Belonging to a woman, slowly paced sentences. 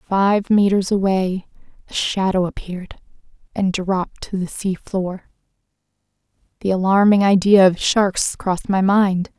Yes: female; slow, 120 wpm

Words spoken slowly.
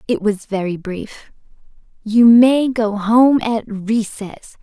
Yes: slow, 130 wpm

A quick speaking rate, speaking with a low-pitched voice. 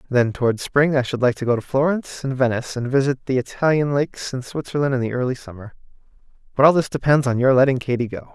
Yes: fast, 230 wpm; low, 130 Hz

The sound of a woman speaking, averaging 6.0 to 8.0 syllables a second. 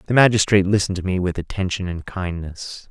No: male; 6.2 syllables/s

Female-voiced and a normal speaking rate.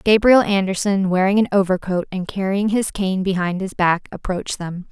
Yes: female; average, 170 wpm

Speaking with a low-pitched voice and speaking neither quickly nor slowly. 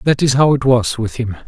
No: low, 125 Hz; fast, 285 wpm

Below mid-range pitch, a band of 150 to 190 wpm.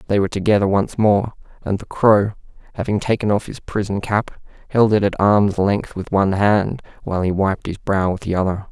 No: low, 100 Hz; fast, 205 wpm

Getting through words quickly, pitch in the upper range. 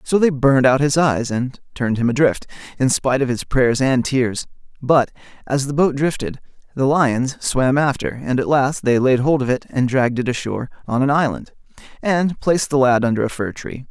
No: fast, 210 wpm; low, 130 Hz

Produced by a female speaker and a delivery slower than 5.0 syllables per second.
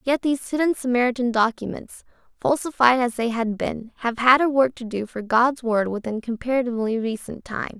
No: female; 5.6 syllables/s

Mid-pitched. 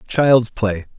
No: low, 115 Hz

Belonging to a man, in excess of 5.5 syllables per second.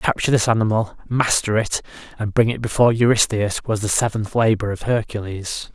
Yes: male; 5.8 syllables/s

